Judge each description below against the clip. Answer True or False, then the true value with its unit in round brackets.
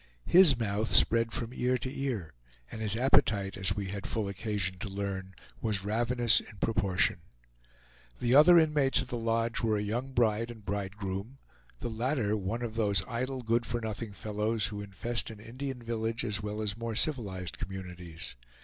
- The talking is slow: False (175 wpm)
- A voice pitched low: True (110 Hz)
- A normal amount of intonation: True (3.0 semitones)